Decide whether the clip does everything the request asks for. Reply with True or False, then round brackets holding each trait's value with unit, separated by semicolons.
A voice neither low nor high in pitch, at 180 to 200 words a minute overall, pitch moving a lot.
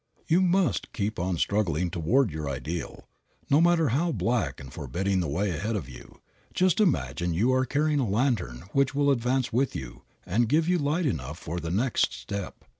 False (110 Hz; 185 wpm; 8.7 semitones)